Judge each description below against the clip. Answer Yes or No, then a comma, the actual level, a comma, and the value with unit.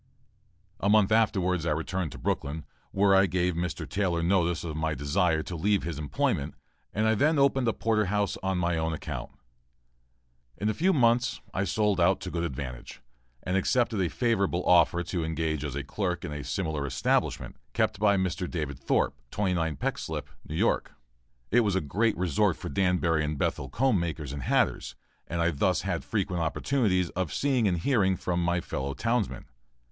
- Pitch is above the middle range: No, very low, 90 Hz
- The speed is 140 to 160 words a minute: No, average, 185 wpm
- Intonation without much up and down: No, average, 4.2 semitones